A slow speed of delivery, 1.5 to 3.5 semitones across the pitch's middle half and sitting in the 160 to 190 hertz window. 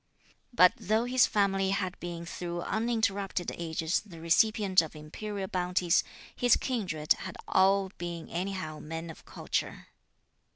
Yes: slow, 130 wpm; average, 3.2 semitones; medium, 185 Hz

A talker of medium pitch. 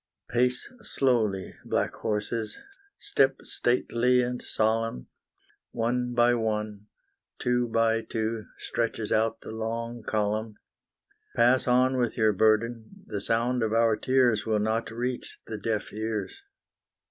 No: low, 115 Hz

